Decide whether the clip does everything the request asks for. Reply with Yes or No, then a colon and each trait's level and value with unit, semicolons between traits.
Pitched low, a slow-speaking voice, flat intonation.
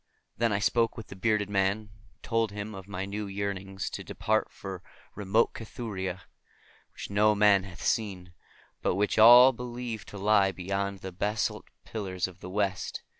No: low, 100 Hz; average, 170 wpm; narrow, 2.1 semitones